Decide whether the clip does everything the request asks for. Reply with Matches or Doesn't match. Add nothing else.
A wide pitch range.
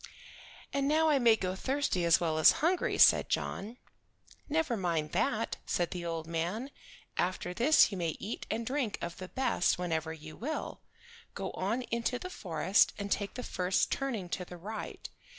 Matches